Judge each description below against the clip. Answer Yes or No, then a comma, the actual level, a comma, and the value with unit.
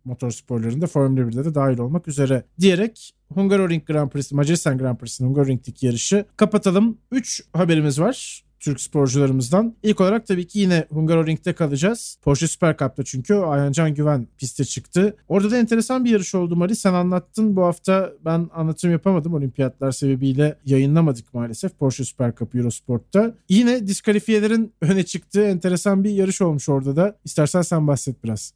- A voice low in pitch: No, medium, 165 Hz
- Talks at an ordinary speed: No, fast, 160 wpm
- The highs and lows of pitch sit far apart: Yes, wide, 6.0 semitones